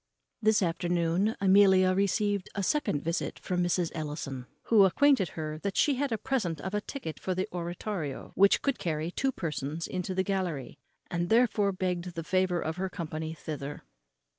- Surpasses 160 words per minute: Yes, average, 170 wpm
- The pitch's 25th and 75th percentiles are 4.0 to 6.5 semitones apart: No, average, 3.4 semitones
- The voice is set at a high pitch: No, medium, 180 Hz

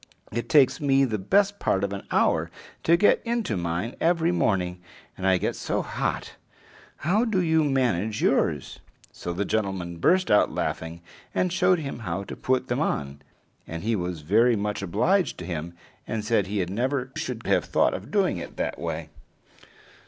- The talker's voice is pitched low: Yes, low, 110 Hz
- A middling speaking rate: Yes, average, 175 wpm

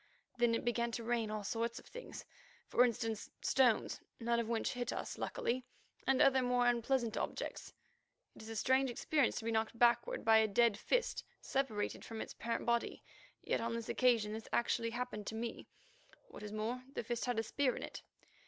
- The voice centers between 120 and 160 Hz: No, high, 235 Hz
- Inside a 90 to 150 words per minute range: No, average, 200 wpm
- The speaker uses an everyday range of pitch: No, narrow, 1.8 semitones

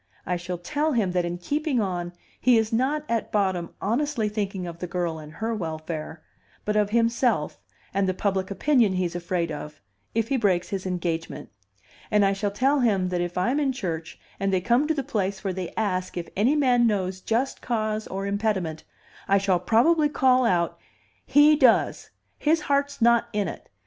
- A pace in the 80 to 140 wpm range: No, average, 190 wpm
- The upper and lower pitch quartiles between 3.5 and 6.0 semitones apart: Yes, average, 5.2 semitones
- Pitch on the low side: No, high, 200 Hz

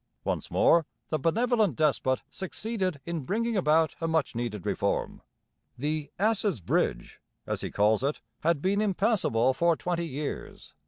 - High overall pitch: No, medium, 165 Hz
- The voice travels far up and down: Yes, wide, 5.9 semitones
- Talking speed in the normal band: Yes, average, 145 wpm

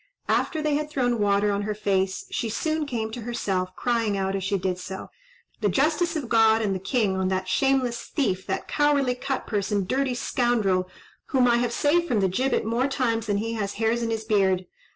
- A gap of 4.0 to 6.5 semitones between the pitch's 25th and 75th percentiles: Yes, average, 4.6 semitones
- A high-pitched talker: Yes, high, 225 Hz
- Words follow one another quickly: Yes, fast, 215 wpm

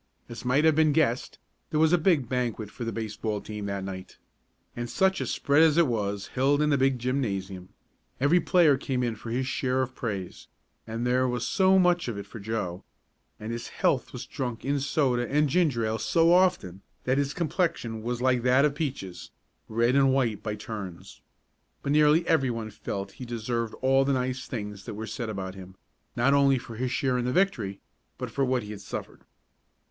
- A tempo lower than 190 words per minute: No, fast, 205 wpm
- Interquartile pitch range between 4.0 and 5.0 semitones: Yes, average, 4.4 semitones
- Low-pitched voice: Yes, low, 125 Hz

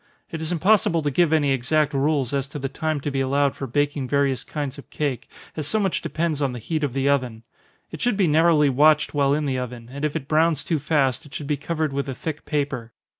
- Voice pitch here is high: No, medium, 145 Hz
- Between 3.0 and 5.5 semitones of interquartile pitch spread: No, narrow, 2.5 semitones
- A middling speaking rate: No, fast, 245 wpm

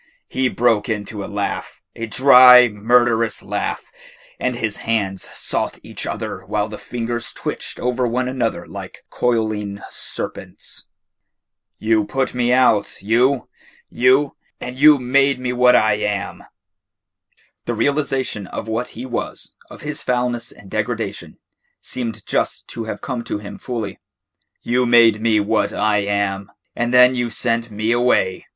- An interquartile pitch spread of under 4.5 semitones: Yes, average, 2.9 semitones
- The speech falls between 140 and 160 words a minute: Yes, average, 145 wpm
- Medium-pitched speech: No, low, 115 Hz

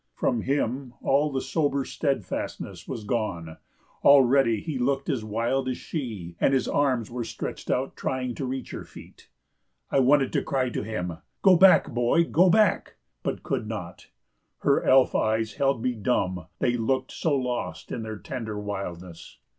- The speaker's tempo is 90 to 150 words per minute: No, average, 165 wpm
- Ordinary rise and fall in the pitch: Yes, average, 3.9 semitones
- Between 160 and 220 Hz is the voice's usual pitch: No, low, 125 Hz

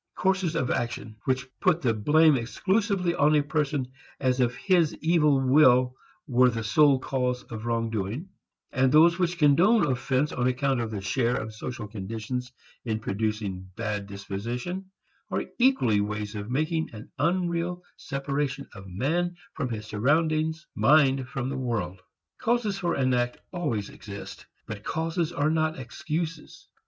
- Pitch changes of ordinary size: No, wide, 5.9 semitones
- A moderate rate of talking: Yes, average, 150 wpm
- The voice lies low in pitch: Yes, low, 130 Hz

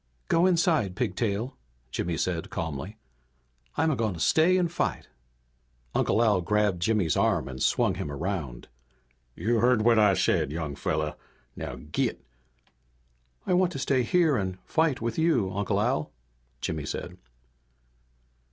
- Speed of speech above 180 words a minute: No, average, 145 wpm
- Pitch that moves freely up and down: Yes, wide, 8.0 semitones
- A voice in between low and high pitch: No, low, 105 Hz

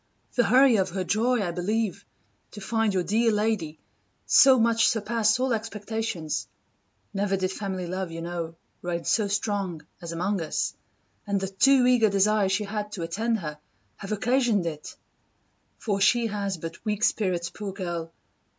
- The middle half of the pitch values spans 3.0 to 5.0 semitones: Yes, average, 3.7 semitones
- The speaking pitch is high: Yes, high, 200 Hz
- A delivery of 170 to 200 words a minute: No, average, 160 wpm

